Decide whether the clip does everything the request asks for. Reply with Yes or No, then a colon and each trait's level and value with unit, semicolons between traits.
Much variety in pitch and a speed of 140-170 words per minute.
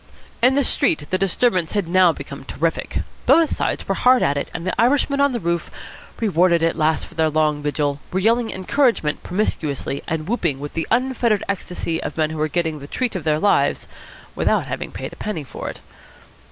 No: wide, 6.6 semitones; average, 200 wpm